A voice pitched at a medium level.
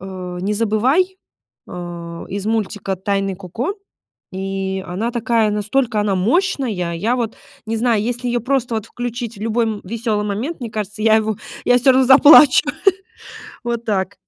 No: high, 220 Hz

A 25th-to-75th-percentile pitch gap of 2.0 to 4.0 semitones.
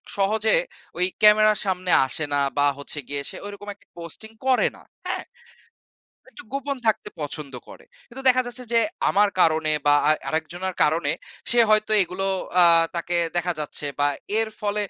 No: average, 5.2 semitones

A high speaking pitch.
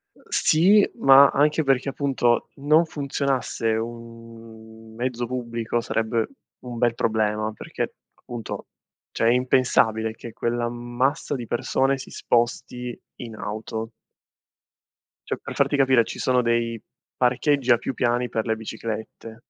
No: low, 120 Hz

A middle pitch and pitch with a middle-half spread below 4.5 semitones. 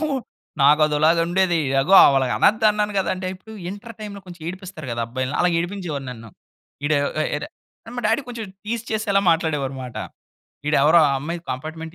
No: medium, 170 Hz; wide, 5.5 semitones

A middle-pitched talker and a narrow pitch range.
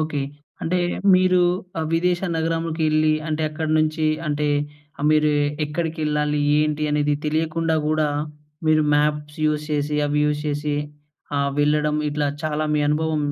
Yes: medium, 155 Hz; narrow, 1.2 semitones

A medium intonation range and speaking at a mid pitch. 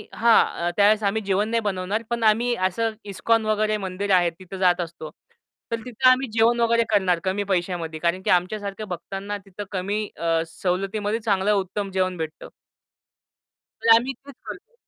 No: average, 3.3 semitones; high, 200 Hz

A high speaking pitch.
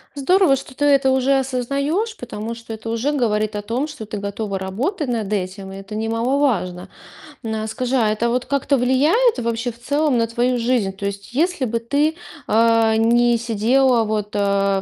Yes: high, 235 Hz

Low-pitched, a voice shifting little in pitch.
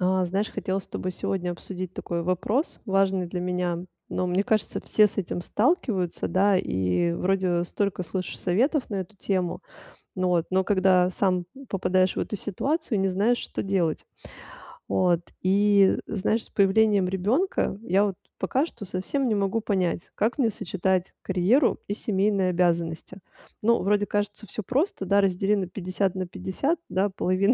No: high, 190 Hz; narrow, 2.3 semitones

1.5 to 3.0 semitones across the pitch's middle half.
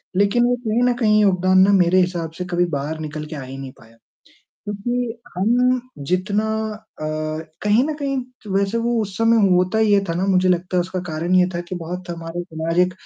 No: average, 4.3 semitones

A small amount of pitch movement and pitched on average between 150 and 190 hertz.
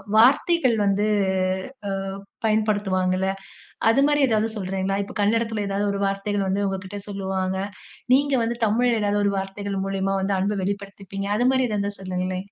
No: narrow, 2.2 semitones; high, 200 Hz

